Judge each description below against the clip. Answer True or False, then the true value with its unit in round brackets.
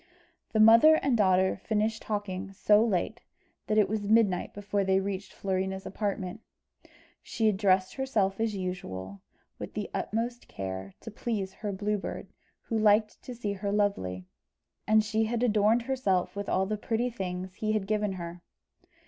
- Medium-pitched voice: False (205 Hz)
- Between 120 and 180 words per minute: True (165 wpm)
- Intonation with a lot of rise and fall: False (2.5 semitones)